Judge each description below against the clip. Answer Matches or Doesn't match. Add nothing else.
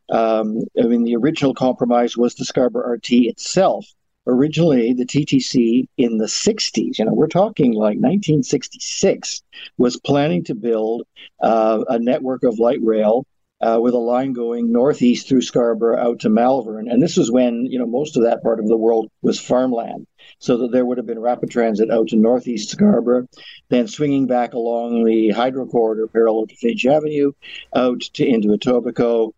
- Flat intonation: Matches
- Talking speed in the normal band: Matches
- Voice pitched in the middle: Doesn't match